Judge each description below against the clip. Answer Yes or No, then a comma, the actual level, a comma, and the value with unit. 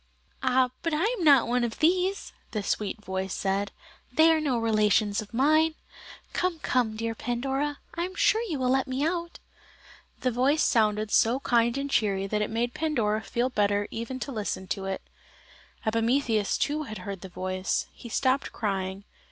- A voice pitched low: No, high, 240 Hz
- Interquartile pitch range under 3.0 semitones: No, average, 5.2 semitones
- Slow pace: No, average, 175 wpm